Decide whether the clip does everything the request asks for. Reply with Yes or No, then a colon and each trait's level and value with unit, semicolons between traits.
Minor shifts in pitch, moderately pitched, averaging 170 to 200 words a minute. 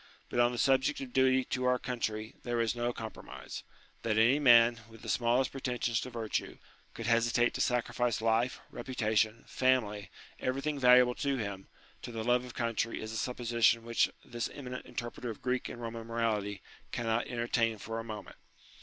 No: narrow, 1.8 semitones; low, 120 Hz; average, 180 wpm